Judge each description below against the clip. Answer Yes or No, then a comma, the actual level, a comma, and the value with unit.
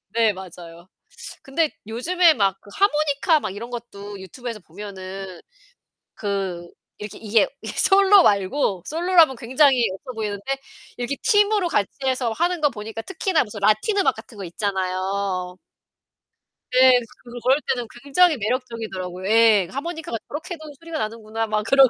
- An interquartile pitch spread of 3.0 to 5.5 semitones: No, wide, 6.7 semitones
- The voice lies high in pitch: Yes, high, 230 Hz